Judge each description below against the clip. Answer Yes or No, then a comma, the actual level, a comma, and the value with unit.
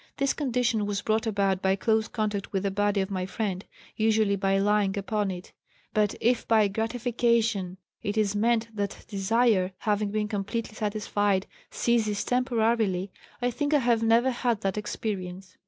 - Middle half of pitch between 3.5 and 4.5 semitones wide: No, narrow, 2.6 semitones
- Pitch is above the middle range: Yes, high, 210 Hz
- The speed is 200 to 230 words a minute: No, average, 160 wpm